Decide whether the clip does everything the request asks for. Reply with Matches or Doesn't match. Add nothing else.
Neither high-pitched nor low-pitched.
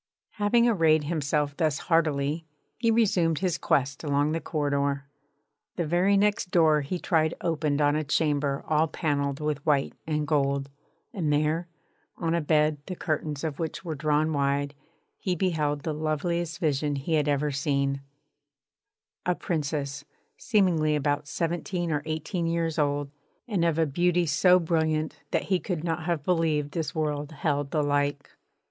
Matches